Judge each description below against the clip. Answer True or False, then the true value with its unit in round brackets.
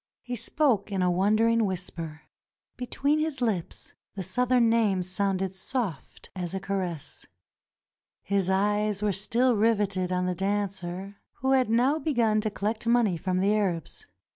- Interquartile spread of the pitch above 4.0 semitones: False (3.7 semitones)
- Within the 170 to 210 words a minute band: False (145 wpm)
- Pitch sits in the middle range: False (200 Hz)